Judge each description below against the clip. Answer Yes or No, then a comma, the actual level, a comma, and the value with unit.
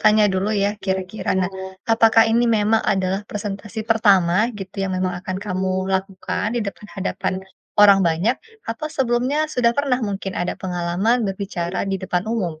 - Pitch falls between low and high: No, high, 195 Hz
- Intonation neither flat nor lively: Yes, average, 3.1 semitones